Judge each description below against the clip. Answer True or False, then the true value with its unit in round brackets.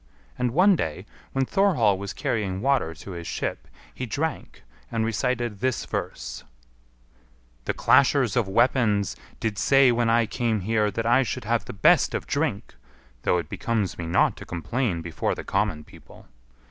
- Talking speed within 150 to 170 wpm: True (165 wpm)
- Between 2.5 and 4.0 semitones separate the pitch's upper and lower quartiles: False (4.5 semitones)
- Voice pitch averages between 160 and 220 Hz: False (115 Hz)